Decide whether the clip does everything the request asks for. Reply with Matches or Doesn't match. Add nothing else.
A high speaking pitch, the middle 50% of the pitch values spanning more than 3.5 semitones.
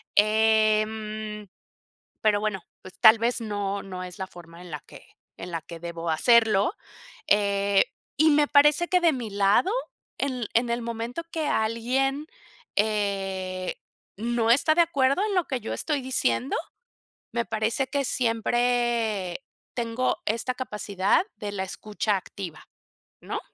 Matches